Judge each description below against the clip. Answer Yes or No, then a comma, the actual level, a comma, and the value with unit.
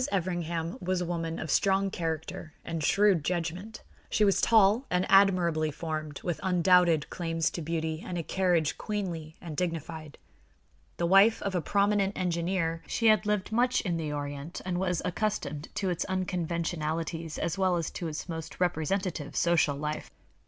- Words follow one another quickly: No, average, 160 wpm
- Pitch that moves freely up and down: No, average, 2.8 semitones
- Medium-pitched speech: Yes, medium, 175 Hz